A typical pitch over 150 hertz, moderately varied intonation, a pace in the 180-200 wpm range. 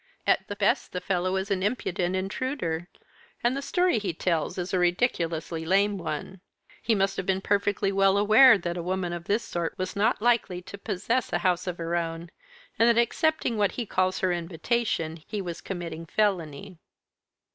Yes: high, 190 Hz; average, 3.2 semitones; average, 185 wpm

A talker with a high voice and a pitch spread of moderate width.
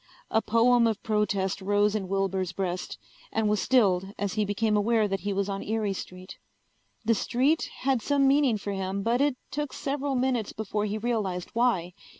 Yes: high, 210 Hz; average, 3.7 semitones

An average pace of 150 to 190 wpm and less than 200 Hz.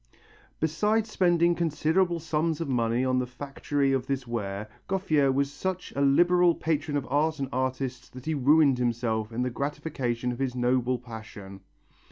Yes: average, 165 wpm; low, 135 Hz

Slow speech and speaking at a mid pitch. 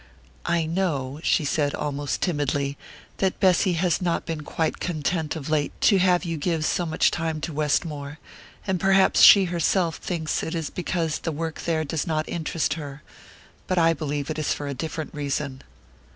No: average, 180 wpm; medium, 160 Hz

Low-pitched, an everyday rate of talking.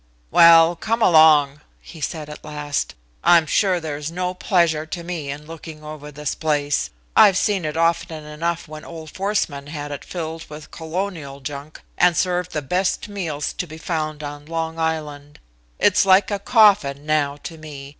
No: medium, 160 Hz; average, 175 wpm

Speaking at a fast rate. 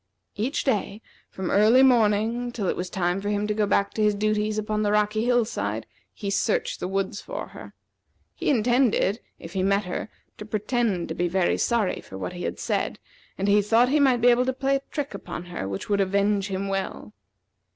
Yes: fast, 215 wpm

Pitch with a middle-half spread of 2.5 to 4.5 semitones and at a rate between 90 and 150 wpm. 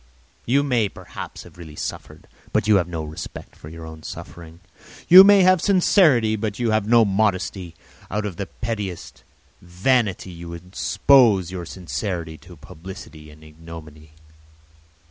No: average, 5.2 semitones; average, 145 wpm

